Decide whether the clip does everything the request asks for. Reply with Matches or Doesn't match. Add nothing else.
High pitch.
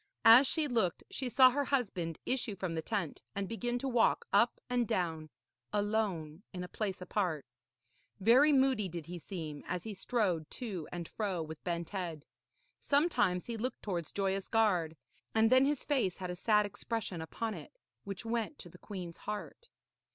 Matches